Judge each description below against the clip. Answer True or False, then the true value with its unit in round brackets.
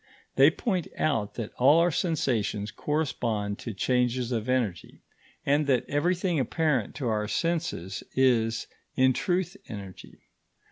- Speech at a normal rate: False (130 wpm)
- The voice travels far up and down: True (6.1 semitones)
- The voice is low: True (130 Hz)